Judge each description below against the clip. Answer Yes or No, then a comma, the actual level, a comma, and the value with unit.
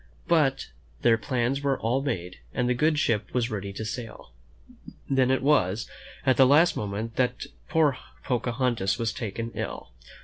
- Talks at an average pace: Yes, average, 160 wpm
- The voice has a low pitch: Yes, low, 125 Hz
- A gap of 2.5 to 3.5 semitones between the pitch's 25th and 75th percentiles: Yes, average, 3.2 semitones